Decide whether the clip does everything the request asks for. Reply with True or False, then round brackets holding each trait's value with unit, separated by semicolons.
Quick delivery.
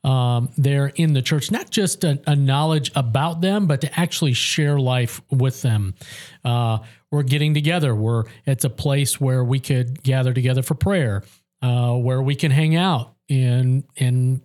False (180 wpm)